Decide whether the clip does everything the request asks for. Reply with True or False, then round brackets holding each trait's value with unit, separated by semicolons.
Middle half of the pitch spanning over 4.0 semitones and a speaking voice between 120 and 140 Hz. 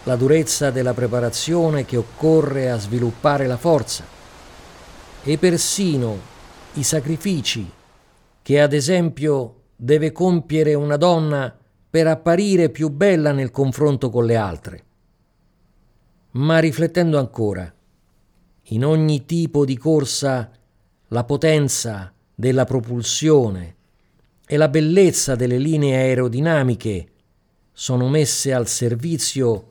True (4.6 semitones; 135 Hz)